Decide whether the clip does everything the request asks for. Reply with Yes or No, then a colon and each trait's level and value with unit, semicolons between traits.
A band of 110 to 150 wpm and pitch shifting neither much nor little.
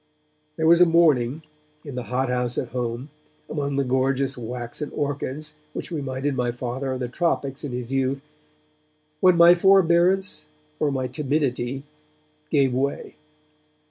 Yes: average, 140 wpm; average, 3.5 semitones